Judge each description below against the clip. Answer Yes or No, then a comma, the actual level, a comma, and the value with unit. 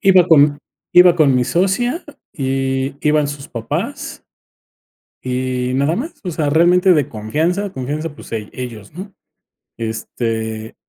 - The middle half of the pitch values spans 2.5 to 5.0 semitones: No, wide, 5.6 semitones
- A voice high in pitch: No, medium, 145 Hz